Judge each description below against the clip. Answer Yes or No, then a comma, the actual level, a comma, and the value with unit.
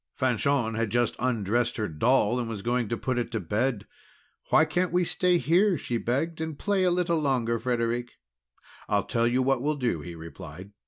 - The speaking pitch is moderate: No, low, 120 Hz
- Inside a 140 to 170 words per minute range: No, average, 195 wpm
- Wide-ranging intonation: No, average, 4.3 semitones